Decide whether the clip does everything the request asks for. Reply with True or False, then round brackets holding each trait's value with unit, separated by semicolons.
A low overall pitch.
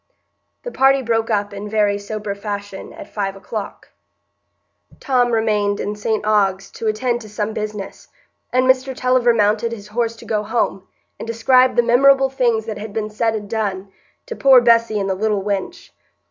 False (220 Hz)